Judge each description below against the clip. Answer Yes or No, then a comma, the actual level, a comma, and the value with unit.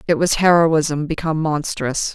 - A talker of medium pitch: Yes, medium, 160 Hz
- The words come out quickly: No, average, 140 wpm